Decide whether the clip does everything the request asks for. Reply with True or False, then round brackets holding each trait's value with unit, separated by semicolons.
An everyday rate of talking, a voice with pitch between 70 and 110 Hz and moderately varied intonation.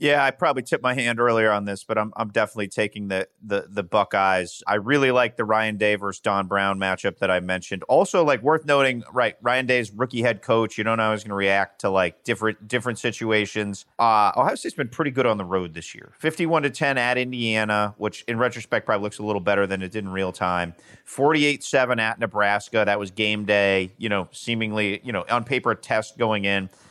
False (230 wpm; 105 Hz; 3.4 semitones)